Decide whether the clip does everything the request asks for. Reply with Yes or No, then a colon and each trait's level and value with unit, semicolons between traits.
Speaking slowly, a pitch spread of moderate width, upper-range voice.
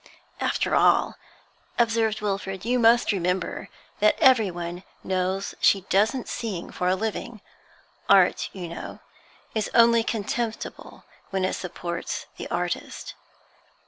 Yes: slow, 115 wpm; average, 3.9 semitones; high, 200 Hz